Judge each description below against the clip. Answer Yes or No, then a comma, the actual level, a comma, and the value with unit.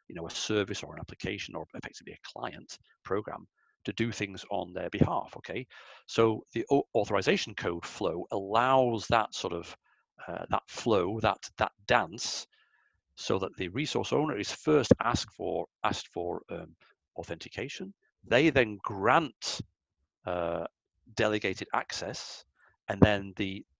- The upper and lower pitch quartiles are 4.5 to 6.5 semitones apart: No, average, 4.0 semitones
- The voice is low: Yes, low, 105 Hz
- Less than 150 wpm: Yes, average, 140 wpm